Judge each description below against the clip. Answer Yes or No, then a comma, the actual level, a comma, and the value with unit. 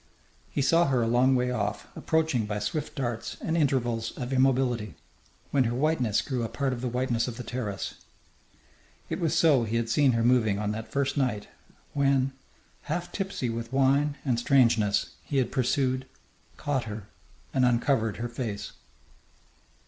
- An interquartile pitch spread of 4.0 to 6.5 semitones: No, average, 3.2 semitones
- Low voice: Yes, low, 125 Hz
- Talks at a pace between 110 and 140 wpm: No, average, 165 wpm